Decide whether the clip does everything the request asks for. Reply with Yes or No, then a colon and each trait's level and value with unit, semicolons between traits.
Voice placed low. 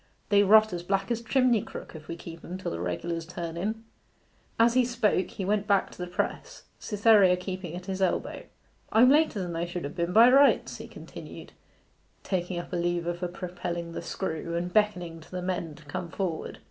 No: medium, 180 Hz